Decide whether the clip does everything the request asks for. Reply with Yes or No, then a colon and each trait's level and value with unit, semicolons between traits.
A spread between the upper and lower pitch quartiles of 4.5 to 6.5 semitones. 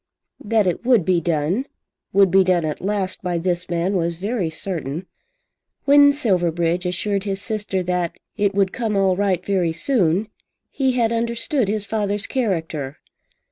No: average, 3.6 semitones